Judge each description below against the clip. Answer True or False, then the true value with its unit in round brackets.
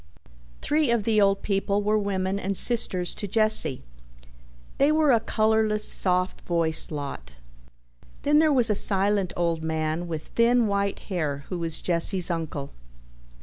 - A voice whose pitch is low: False (195 Hz)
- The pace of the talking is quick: False (145 wpm)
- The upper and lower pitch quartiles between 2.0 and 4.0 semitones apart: False (4.4 semitones)